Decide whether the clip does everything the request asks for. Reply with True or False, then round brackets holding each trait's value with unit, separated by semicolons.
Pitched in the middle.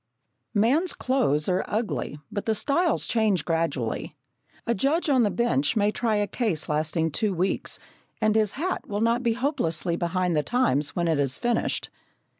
False (210 Hz)